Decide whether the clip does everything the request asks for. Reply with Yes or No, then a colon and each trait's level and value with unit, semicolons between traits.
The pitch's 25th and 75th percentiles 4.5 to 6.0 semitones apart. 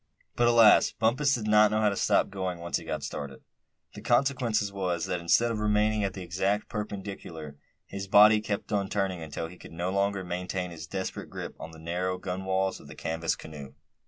No: average, 3.3 semitones